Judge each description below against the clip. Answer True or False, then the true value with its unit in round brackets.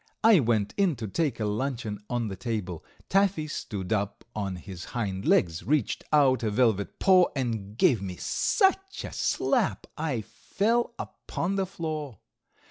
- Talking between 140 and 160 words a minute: True (155 wpm)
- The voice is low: True (120 Hz)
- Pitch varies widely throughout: True (7.9 semitones)